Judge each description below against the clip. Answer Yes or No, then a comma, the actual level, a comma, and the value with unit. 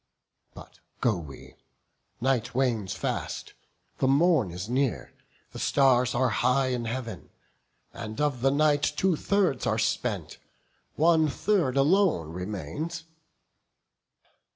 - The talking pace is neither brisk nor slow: No, slow, 115 wpm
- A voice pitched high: No, low, 130 Hz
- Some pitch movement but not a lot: Yes, average, 4.7 semitones